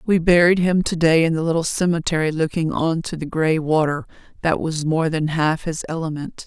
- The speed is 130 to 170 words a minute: No, fast, 205 wpm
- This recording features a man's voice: No, female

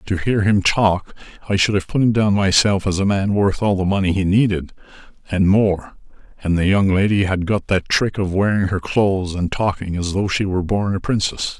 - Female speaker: No, male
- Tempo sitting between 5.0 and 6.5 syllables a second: Yes, 5.2 syllables/s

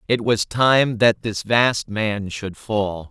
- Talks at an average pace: Yes, average, 175 wpm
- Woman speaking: No, male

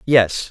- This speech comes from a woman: No, male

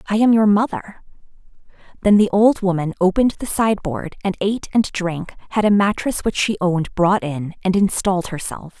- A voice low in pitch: No, high, 195 Hz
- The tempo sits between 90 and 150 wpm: No, average, 175 wpm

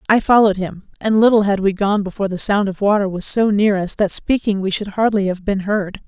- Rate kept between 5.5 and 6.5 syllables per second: Yes, 5.8 syllables/s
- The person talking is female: Yes, female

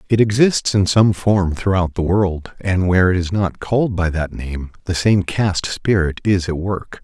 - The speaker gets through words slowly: No, fast, 205 wpm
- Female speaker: No, male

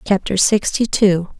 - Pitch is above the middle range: Yes, high, 195 Hz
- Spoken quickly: No, slow, 130 wpm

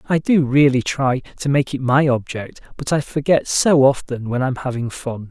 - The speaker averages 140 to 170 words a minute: No, fast, 205 wpm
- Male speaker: Yes, male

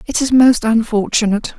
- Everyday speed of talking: Yes, average, 150 wpm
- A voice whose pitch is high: Yes, high, 230 Hz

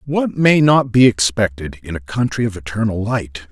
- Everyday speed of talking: Yes, average, 190 wpm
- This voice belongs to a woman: No, male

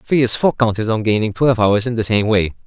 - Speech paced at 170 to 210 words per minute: No, fast, 245 wpm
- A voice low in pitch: Yes, low, 110 Hz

